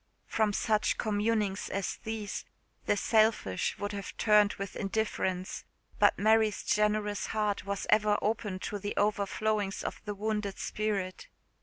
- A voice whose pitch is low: No, high, 210 Hz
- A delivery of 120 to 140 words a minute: Yes, slow, 135 wpm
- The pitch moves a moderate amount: No, narrow, 1.3 semitones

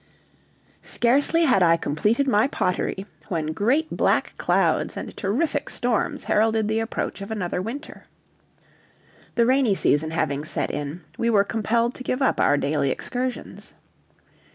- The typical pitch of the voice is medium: No, high, 220 Hz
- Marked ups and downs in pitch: Yes, wide, 5.9 semitones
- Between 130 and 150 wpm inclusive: Yes, average, 140 wpm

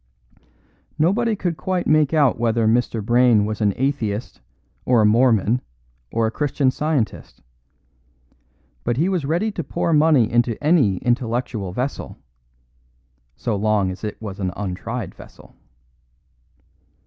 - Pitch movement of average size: No, wide, 5.7 semitones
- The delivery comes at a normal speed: No, slow, 130 wpm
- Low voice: Yes, low, 120 Hz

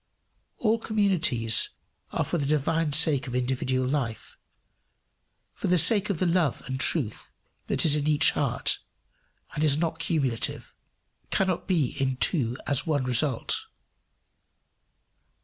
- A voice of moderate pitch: Yes, medium, 150 Hz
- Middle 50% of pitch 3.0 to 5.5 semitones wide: Yes, average, 4.5 semitones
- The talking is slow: Yes, slow, 130 wpm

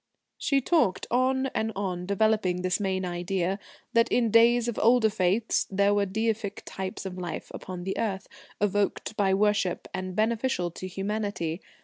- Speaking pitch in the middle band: No, high, 200 Hz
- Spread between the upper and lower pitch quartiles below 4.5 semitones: Yes, average, 3.1 semitones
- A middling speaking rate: Yes, average, 155 wpm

